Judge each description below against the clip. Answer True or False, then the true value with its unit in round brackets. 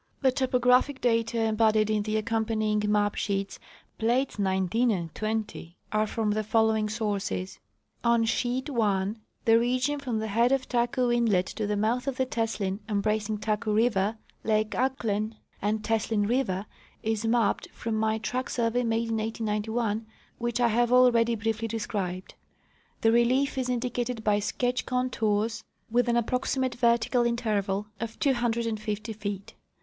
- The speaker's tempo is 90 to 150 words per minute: True (145 wpm)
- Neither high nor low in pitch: False (225 Hz)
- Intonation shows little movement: True (2.3 semitones)